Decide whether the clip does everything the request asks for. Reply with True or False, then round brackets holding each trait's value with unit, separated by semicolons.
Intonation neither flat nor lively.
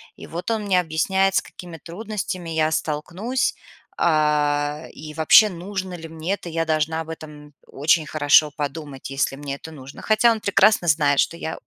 True (3.4 semitones)